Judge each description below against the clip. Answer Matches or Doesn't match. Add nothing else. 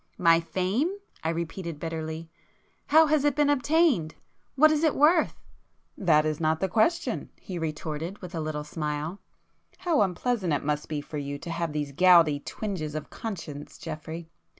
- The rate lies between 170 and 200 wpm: Doesn't match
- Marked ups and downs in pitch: Matches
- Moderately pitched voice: Matches